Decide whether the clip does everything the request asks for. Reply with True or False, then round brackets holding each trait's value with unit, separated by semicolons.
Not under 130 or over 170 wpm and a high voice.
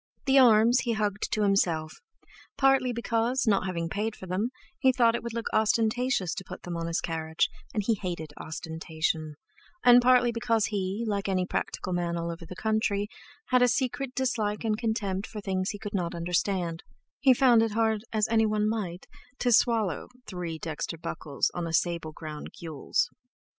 False (180 wpm; 205 Hz)